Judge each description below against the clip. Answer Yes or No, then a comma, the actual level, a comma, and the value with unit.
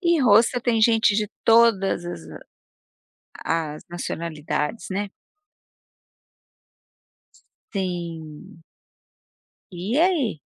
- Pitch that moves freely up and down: Yes, wide, 5.7 semitones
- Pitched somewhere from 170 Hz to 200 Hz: Yes, high, 195 Hz